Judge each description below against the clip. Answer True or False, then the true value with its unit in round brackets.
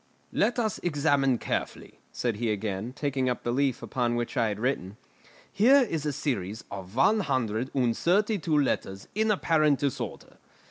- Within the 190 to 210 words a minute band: False (170 wpm)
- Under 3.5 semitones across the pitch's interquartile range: False (5.2 semitones)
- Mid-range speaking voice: False (130 Hz)